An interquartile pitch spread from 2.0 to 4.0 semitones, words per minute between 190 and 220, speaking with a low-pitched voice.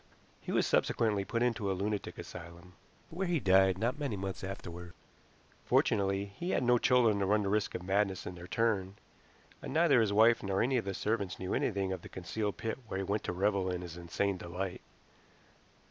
Yes: average, 3.1 semitones; average, 200 wpm; low, 100 Hz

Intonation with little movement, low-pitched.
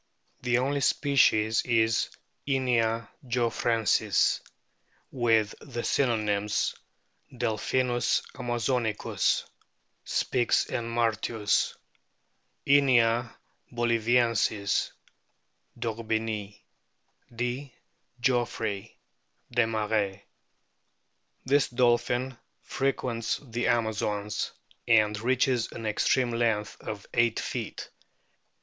Yes: narrow, 2.0 semitones; low, 115 Hz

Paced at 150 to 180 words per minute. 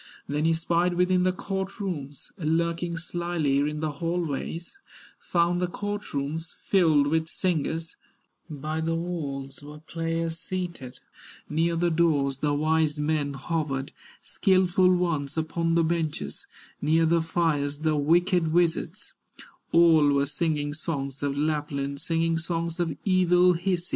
No: average, 140 wpm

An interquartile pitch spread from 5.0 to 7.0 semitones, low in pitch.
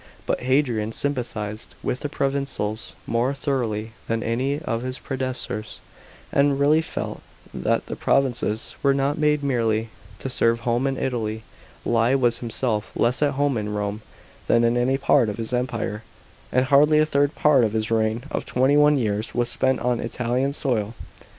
No: average, 3.4 semitones; low, 125 Hz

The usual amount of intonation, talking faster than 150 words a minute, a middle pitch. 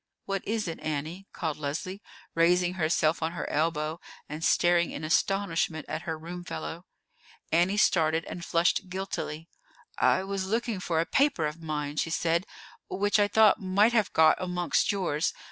Yes: average, 3.4 semitones; average, 160 wpm; medium, 170 Hz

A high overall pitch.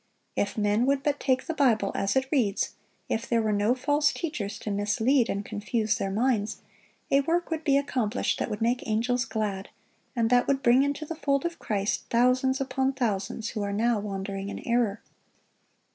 Yes: high, 235 Hz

